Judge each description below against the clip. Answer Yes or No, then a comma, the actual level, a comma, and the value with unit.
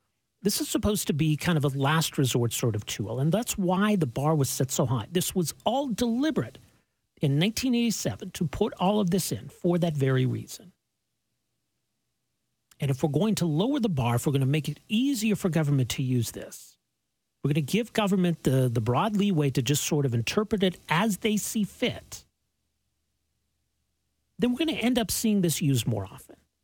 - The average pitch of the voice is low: No, medium, 155 Hz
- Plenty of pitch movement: Yes, wide, 8.5 semitones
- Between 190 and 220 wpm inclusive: Yes, average, 200 wpm